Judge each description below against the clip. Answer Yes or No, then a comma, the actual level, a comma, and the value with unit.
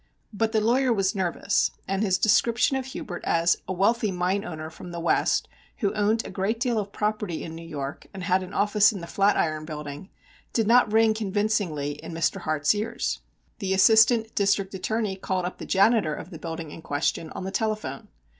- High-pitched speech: Yes, high, 195 Hz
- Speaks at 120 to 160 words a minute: No, average, 195 wpm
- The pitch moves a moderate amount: Yes, average, 4.4 semitones